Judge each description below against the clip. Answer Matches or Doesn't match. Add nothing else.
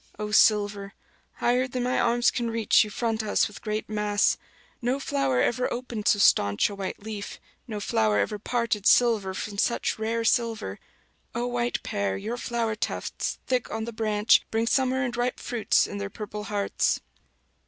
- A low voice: Doesn't match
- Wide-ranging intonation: Doesn't match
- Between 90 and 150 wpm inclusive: Doesn't match